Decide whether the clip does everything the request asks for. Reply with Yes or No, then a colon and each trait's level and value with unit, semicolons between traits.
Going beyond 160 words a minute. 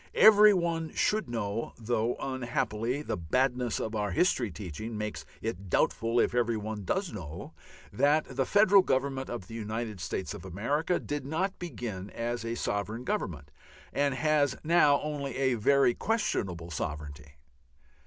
No: average, 150 wpm